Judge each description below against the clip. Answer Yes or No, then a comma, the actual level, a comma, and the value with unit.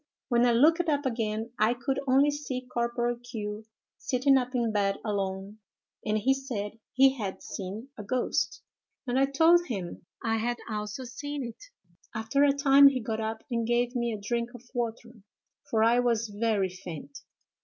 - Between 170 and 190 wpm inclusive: Yes, average, 175 wpm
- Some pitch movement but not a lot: Yes, average, 3.4 semitones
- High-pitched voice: Yes, high, 235 Hz